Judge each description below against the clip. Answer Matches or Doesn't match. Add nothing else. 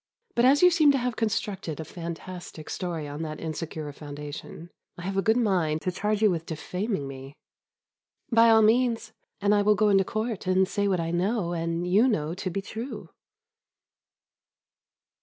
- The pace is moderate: Matches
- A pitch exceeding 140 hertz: Matches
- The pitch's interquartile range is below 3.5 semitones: Doesn't match